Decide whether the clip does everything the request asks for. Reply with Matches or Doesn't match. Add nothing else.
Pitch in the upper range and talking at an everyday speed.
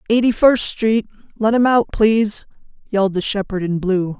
Matches